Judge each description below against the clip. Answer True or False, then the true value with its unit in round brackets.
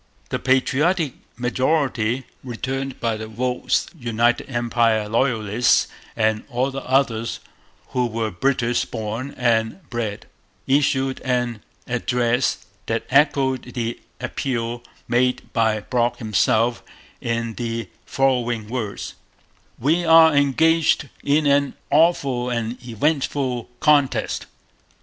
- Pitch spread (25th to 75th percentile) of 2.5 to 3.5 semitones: True (2.8 semitones)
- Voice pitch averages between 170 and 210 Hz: False (125 Hz)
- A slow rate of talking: True (105 wpm)